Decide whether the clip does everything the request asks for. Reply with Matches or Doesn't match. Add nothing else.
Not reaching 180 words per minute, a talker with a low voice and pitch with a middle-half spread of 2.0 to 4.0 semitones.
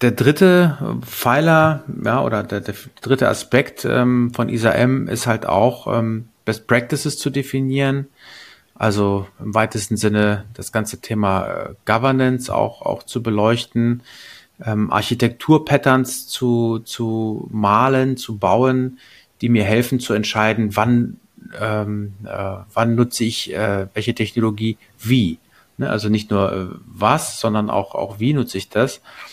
Matches